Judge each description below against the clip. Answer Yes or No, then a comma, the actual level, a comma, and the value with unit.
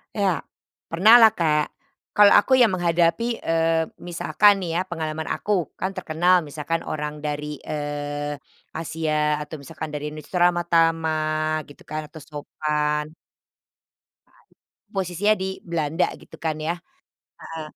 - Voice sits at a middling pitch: Yes, medium, 160 Hz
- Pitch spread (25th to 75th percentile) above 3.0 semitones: No, average, 2.7 semitones